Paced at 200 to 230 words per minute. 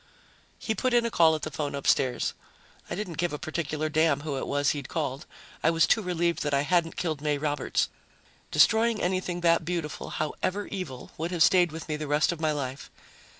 Yes: fast, 205 wpm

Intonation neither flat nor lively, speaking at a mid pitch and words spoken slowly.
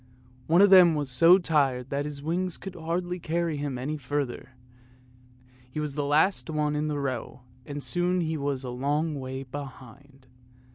No: average, 3.4 semitones; medium, 145 Hz; average, 175 wpm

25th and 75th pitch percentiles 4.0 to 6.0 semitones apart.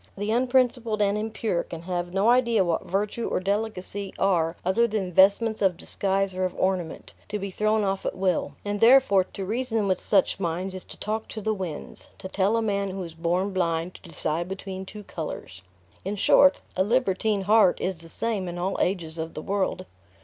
No: average, 2.7 semitones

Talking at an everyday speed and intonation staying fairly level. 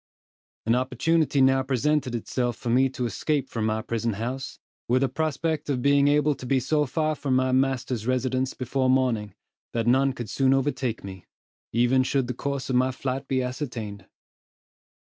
Yes: average, 175 wpm; narrow, 2.1 semitones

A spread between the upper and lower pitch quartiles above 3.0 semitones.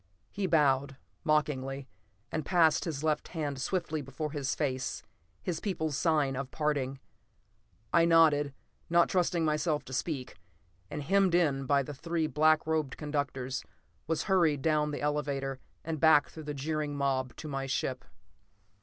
No: average, 2.7 semitones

